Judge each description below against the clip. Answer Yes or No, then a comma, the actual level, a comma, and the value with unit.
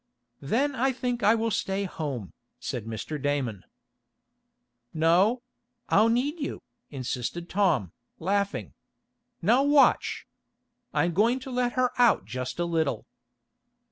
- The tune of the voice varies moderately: No, wide, 9.0 semitones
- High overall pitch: Yes, high, 195 Hz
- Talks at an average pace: No, slow, 120 wpm